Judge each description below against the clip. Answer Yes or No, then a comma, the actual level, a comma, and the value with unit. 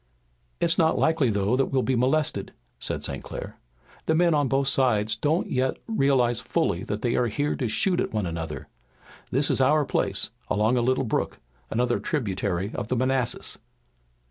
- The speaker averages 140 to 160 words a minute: No, average, 175 wpm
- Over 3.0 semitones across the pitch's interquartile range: Yes, average, 4.9 semitones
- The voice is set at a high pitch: No, low, 130 Hz